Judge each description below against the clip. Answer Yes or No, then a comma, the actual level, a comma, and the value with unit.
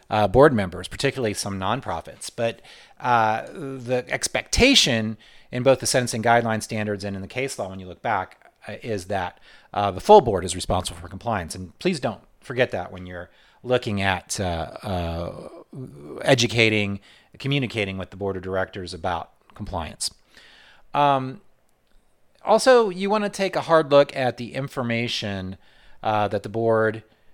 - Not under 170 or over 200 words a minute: No, average, 160 wpm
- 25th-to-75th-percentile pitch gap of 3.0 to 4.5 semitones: No, wide, 5.4 semitones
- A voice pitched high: No, low, 110 Hz